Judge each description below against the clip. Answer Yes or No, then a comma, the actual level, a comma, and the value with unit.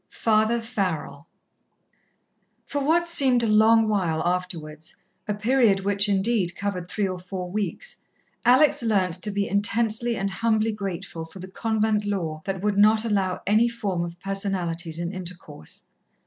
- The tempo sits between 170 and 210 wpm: No, average, 150 wpm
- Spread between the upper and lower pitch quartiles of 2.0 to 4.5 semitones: Yes, average, 3.4 semitones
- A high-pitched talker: Yes, high, 200 Hz